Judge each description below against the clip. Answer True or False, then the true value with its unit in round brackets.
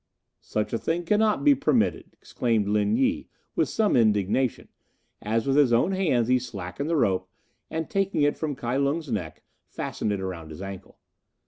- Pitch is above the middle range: False (125 Hz)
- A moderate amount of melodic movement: False (7.9 semitones)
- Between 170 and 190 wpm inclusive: True (175 wpm)